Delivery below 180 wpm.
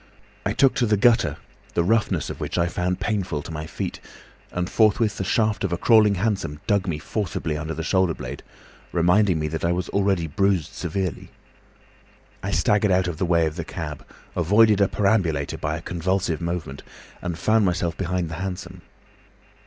No: average, 185 wpm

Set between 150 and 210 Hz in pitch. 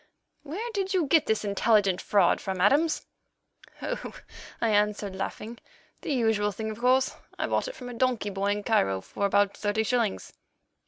No: high, 220 Hz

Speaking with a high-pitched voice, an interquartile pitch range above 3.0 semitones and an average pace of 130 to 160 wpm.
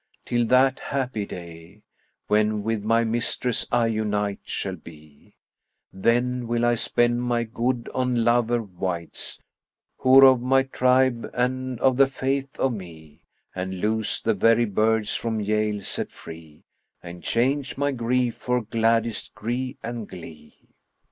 No: low, 115 Hz; average, 3.4 semitones; average, 150 wpm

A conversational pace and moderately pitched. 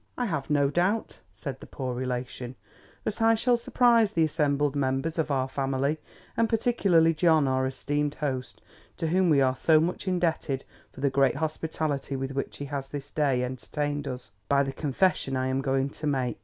Yes: average, 185 wpm; medium, 145 Hz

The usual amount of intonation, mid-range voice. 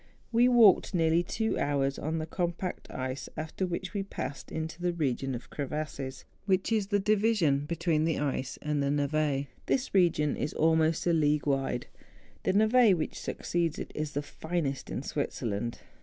Yes: average, 4.2 semitones; medium, 160 Hz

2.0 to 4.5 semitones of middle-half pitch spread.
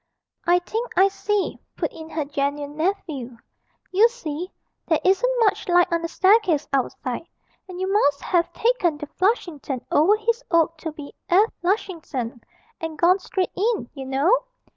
No: average, 5.1 semitones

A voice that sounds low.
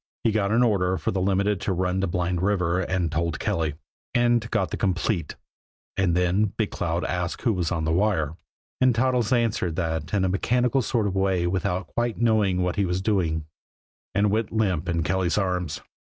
Yes: very low, 95 Hz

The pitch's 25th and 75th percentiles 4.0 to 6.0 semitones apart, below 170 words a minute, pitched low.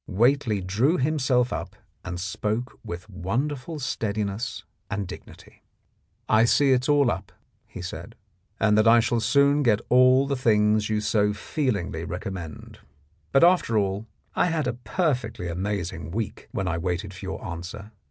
Yes: average, 5.0 semitones; average, 160 wpm; low, 110 Hz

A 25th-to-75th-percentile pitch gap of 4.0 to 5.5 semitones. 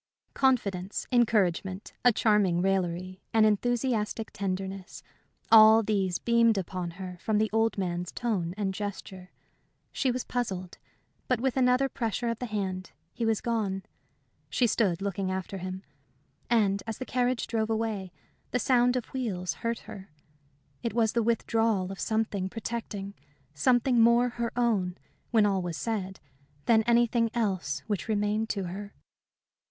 No: average, 3.6 semitones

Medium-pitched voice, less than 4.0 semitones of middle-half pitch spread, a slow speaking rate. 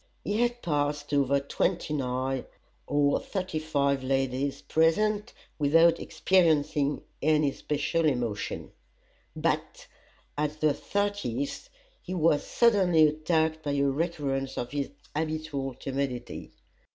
Yes: medium, 150 Hz; average, 2.8 semitones; slow, 115 wpm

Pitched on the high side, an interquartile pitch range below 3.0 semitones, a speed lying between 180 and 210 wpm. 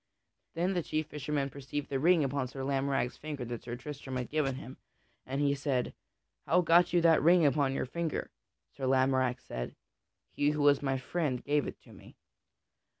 No: medium, 140 Hz; narrow, 2.6 semitones; average, 185 wpm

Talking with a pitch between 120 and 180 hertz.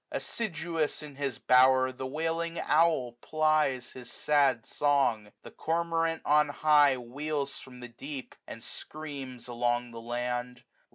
Yes: medium, 140 Hz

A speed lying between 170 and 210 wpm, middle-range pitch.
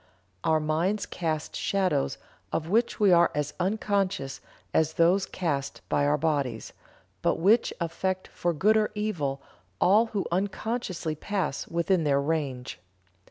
No: slow, 135 wpm; medium, 170 Hz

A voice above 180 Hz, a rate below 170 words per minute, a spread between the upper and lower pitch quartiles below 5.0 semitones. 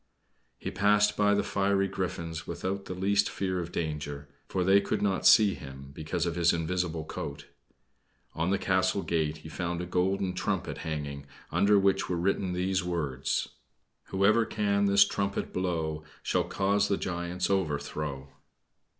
No: very low, 90 Hz; average, 155 wpm; average, 3.7 semitones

